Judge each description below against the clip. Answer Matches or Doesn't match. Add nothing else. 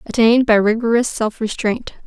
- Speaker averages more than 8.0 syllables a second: Doesn't match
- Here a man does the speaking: Doesn't match